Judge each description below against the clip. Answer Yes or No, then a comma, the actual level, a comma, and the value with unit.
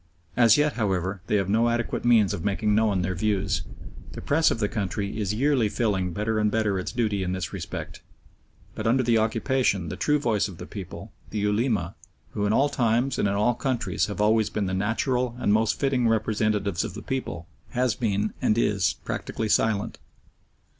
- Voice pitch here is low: Yes, low, 110 Hz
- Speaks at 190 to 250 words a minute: Yes, average, 195 wpm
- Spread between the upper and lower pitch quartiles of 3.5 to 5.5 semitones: No, average, 2.9 semitones